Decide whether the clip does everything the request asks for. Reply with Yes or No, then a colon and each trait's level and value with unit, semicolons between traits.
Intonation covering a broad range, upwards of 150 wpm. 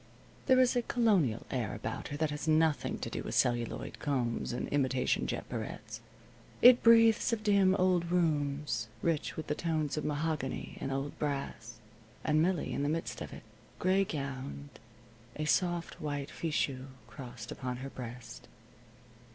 No: average, 4.5 semitones; average, 160 wpm